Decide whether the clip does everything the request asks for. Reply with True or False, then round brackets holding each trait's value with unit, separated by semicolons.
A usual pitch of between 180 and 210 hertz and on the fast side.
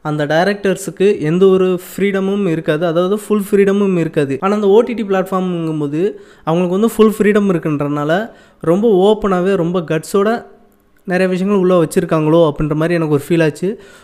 True (185 Hz; 140 wpm)